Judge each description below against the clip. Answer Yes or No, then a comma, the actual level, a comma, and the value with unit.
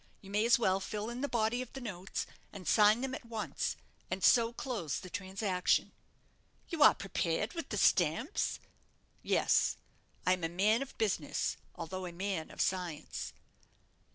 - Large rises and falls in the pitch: No, average, 4.1 semitones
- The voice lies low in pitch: No, high, 205 Hz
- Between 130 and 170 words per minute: Yes, average, 165 wpm